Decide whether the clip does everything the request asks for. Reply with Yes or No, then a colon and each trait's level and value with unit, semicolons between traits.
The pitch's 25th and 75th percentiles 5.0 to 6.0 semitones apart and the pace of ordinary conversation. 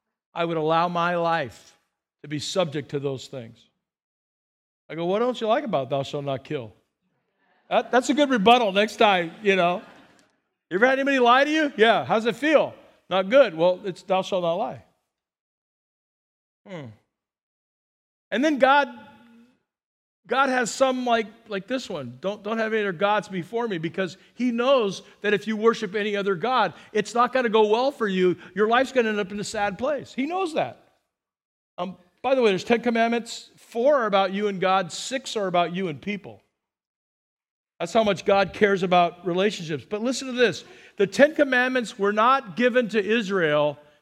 Yes: wide, 5.5 semitones; average, 190 wpm